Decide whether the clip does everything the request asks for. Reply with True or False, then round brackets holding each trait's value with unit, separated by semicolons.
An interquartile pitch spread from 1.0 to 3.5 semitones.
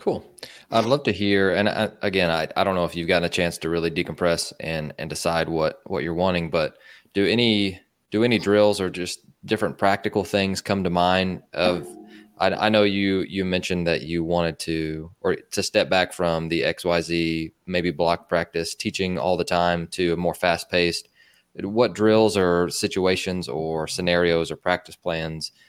True (2.8 semitones)